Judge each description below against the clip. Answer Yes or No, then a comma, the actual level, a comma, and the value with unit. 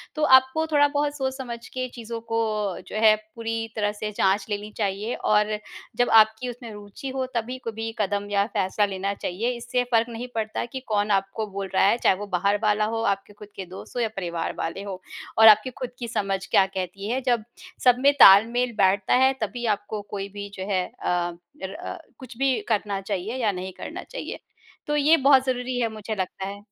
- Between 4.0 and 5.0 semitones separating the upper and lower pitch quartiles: No, average, 3.6 semitones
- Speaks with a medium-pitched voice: No, high, 215 Hz